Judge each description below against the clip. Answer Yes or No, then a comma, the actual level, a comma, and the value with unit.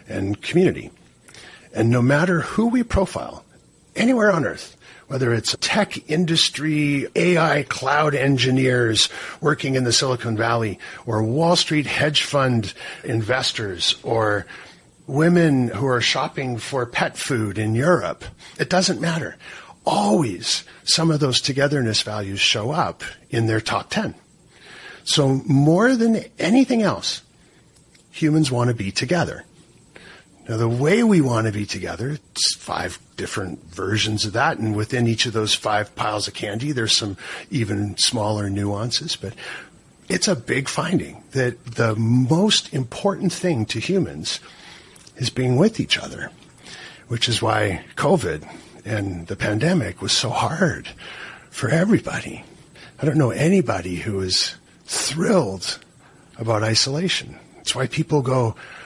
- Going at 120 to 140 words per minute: Yes, slow, 135 wpm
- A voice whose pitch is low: Yes, low, 125 Hz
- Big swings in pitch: Yes, wide, 6.0 semitones